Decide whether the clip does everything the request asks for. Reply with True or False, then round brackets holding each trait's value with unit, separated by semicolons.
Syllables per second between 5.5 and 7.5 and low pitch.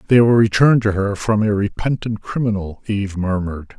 True (6.0 syllables/s; 105 Hz)